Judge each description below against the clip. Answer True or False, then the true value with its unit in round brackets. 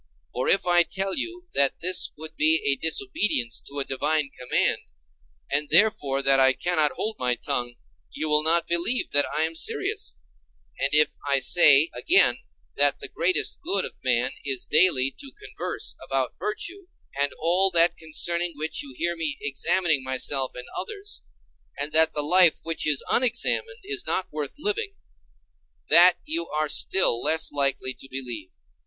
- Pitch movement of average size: False (5.7 semitones)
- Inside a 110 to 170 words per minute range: True (160 wpm)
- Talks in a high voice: False (160 Hz)